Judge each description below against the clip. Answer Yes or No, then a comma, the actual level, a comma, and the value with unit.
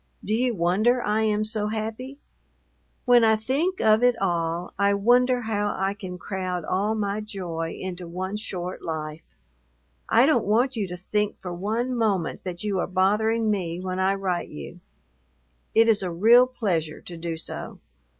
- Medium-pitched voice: No, high, 205 Hz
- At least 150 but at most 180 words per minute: Yes, average, 170 wpm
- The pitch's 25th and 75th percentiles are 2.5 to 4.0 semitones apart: Yes, average, 3.7 semitones